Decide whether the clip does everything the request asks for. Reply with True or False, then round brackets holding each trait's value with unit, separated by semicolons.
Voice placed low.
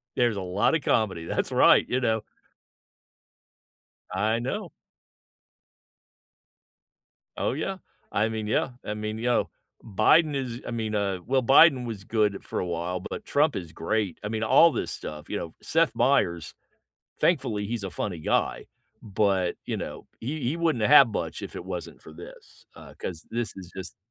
True (110 Hz)